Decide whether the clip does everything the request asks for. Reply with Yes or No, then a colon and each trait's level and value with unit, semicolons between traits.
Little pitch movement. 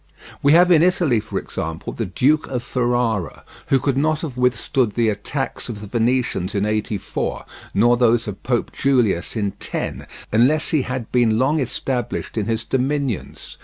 No: average, 3.8 semitones